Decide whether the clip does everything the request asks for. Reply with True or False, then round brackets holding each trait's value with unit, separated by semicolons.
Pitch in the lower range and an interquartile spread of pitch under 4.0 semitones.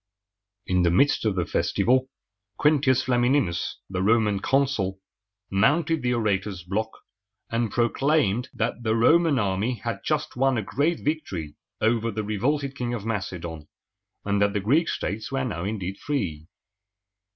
False (115 Hz; 5.5 semitones)